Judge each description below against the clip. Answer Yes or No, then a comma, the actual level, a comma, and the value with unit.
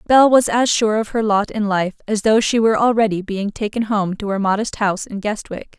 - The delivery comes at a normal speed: No, fast, 240 wpm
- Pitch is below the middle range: No, high, 210 Hz